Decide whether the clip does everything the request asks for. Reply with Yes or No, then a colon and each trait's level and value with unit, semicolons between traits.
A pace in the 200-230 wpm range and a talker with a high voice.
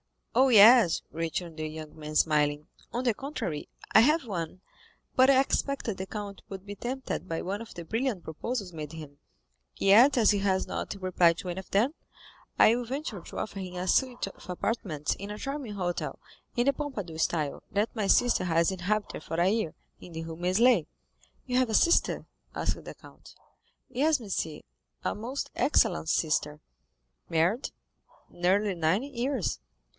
No: average, 170 wpm; high, 200 Hz